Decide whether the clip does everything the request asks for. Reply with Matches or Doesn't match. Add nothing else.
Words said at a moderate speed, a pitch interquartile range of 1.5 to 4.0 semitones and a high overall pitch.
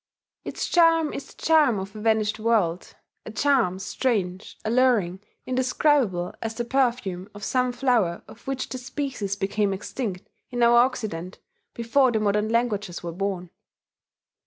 Doesn't match